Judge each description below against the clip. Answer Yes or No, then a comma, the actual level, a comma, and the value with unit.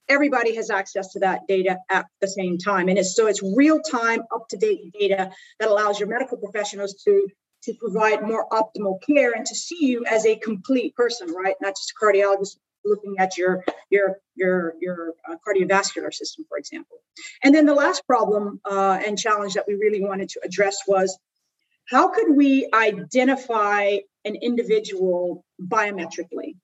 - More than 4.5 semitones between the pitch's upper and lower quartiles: No, average, 3.7 semitones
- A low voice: No, high, 205 Hz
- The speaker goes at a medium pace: Yes, average, 170 wpm